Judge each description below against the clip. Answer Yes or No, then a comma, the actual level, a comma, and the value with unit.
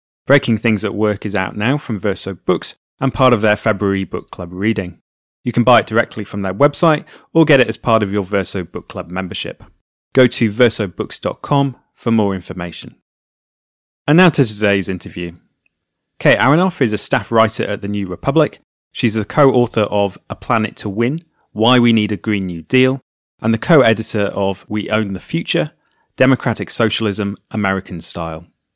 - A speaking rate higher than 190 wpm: No, average, 180 wpm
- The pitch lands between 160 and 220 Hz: No, low, 105 Hz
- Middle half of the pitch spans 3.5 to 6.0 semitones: Yes, average, 4.1 semitones